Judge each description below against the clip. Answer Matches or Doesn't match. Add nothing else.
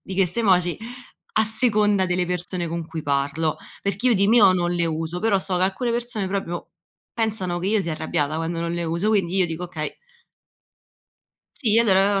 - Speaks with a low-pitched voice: Doesn't match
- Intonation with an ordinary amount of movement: Matches